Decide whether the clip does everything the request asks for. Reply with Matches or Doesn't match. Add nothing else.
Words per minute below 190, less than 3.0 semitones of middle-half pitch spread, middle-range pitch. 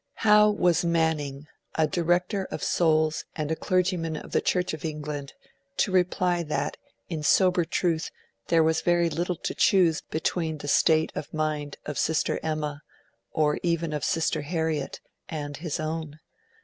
Matches